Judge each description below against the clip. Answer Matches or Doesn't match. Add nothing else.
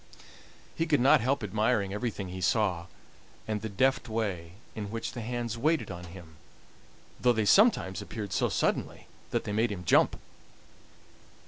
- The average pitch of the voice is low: Matches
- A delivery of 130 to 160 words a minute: Matches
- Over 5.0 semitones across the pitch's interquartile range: Doesn't match